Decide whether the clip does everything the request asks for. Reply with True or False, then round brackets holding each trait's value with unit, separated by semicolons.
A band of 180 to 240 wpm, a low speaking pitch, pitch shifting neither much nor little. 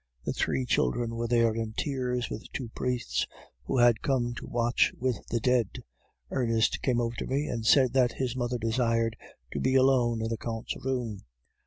False (185 wpm; 120 Hz; 1.9 semitones)